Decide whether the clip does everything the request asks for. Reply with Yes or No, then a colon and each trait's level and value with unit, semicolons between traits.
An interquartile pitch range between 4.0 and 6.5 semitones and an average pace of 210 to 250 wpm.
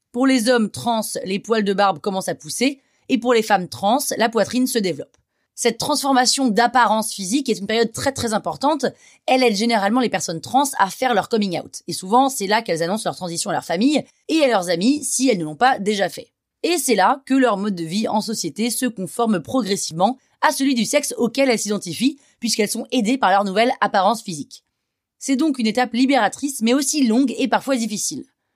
Yes: average, 4.6 semitones; average, 215 wpm